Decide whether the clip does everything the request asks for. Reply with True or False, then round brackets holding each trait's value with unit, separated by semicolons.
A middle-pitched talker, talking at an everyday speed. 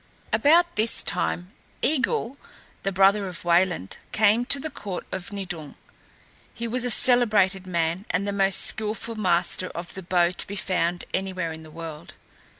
False (195 Hz; 160 wpm)